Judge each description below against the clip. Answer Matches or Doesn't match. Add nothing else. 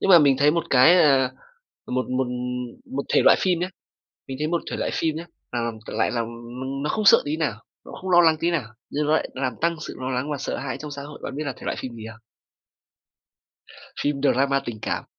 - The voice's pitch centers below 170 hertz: Matches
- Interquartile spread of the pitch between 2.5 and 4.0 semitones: Matches